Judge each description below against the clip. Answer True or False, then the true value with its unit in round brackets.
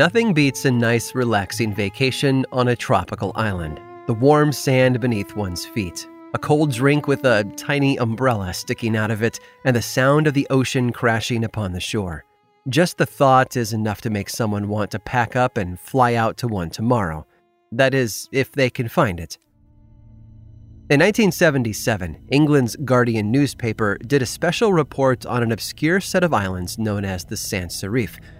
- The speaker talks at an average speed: True (175 wpm)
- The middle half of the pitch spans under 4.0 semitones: False (4.5 semitones)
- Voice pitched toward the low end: True (120 Hz)